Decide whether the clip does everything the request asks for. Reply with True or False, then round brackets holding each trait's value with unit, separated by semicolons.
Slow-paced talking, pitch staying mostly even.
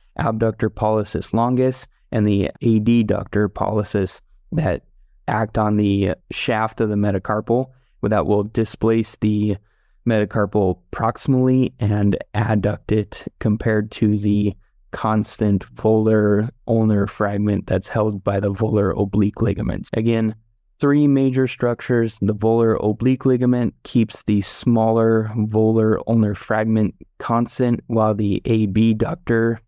True (115 wpm; 1.8 semitones)